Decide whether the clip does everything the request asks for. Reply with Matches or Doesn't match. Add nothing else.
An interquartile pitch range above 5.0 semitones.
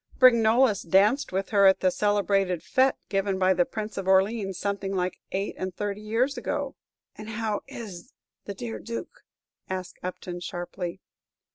Doesn't match